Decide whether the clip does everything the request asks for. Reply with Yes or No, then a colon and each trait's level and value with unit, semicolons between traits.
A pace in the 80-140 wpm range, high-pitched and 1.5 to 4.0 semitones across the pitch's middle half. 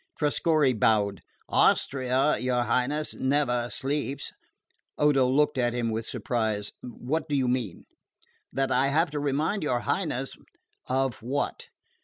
No: slow, 135 wpm; low, 130 Hz; average, 3.2 semitones